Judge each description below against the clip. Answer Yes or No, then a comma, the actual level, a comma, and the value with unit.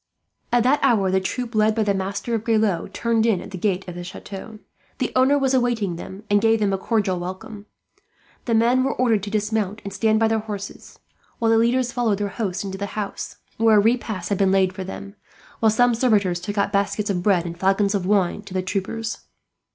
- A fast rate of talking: Yes, fast, 225 wpm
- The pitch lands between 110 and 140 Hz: No, high, 210 Hz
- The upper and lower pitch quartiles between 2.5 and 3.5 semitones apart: Yes, average, 2.8 semitones